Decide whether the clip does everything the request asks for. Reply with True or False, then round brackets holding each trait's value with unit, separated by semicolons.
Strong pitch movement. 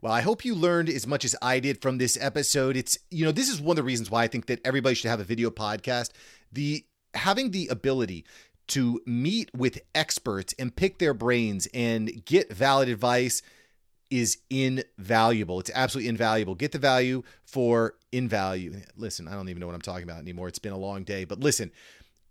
False (3.8 semitones)